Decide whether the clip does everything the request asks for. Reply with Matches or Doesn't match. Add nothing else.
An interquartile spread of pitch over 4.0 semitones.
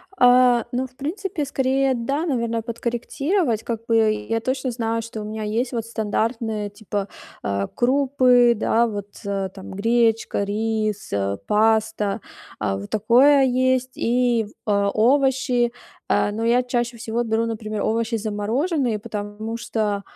Doesn't match